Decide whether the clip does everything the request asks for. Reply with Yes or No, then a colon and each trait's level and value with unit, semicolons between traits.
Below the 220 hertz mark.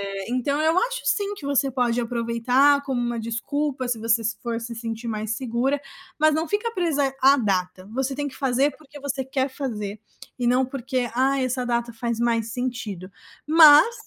No: very high, 255 Hz